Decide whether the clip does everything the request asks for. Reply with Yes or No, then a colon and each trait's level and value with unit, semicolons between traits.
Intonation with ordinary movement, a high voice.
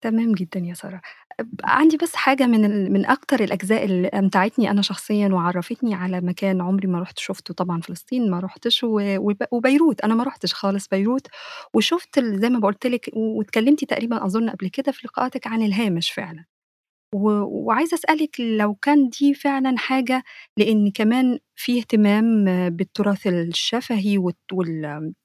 Yes: average, 4.5 semitones; high, 215 Hz